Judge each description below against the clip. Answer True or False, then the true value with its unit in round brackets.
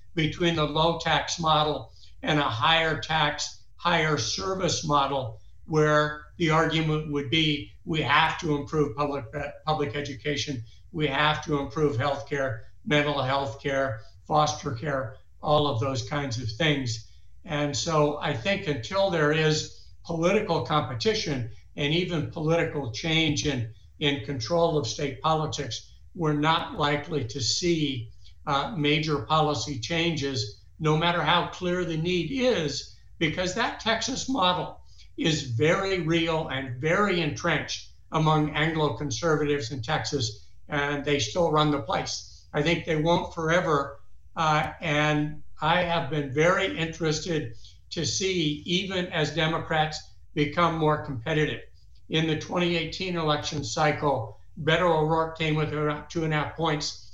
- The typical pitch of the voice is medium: True (150 Hz)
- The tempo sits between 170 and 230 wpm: False (140 wpm)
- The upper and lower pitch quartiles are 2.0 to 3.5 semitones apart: True (2.6 semitones)